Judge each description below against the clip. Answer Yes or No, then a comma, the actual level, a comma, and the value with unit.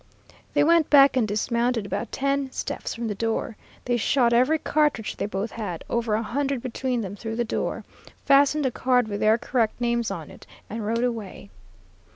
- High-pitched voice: Yes, high, 235 Hz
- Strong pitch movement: No, average, 3.3 semitones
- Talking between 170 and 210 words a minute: Yes, average, 190 wpm